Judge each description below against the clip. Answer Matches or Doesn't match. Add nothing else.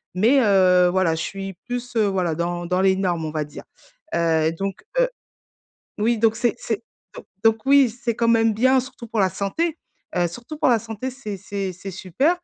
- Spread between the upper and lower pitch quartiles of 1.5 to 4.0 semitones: Doesn't match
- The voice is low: Doesn't match